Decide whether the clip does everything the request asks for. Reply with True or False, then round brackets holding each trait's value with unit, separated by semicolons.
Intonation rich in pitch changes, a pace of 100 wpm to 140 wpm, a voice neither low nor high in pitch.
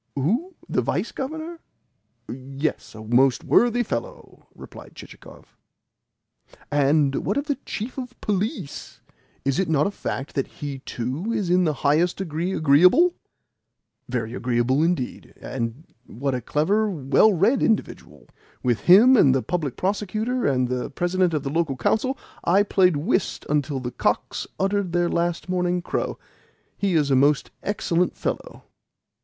False (6.8 semitones; 150 wpm; 170 Hz)